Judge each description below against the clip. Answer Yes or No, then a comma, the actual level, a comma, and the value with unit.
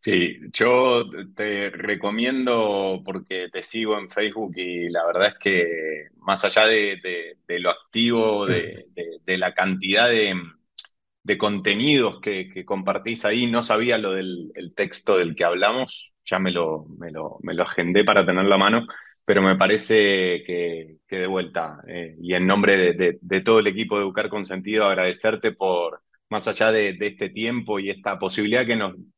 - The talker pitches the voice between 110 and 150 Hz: No, low, 100 Hz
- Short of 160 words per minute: No, average, 180 wpm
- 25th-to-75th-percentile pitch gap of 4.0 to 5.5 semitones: No, average, 3.2 semitones